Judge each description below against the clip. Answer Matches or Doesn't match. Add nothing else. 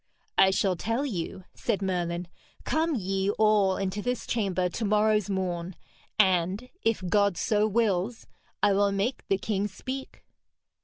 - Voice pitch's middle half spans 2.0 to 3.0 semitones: Matches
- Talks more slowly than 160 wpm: Matches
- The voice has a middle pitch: Doesn't match